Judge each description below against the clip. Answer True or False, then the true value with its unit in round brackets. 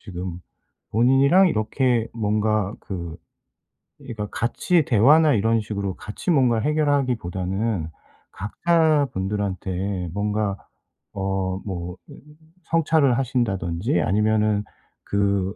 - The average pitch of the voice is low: True (105 Hz)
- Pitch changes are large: False (4.8 semitones)